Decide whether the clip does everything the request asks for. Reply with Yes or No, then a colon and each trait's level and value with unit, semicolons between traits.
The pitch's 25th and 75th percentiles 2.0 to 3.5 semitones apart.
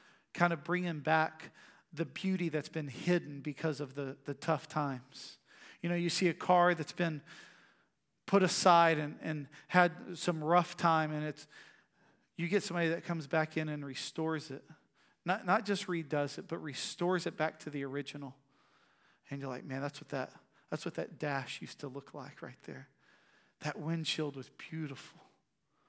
Yes: average, 3.1 semitones